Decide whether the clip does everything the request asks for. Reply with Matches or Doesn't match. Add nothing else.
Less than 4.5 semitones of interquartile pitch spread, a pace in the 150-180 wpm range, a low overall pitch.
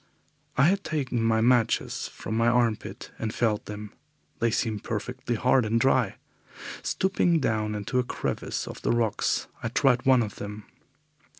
Matches